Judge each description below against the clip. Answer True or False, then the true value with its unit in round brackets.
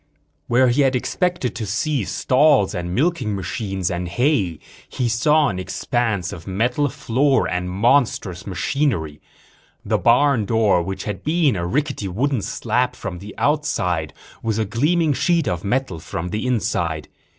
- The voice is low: True (115 Hz)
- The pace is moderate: True (150 wpm)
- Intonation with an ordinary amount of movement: False (6.8 semitones)